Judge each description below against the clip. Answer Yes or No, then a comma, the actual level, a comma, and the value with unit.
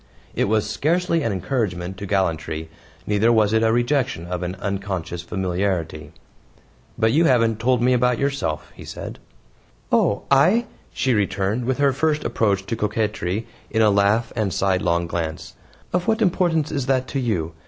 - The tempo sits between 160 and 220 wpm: Yes, average, 165 wpm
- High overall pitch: No, low, 110 Hz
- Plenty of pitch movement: Yes, wide, 5.7 semitones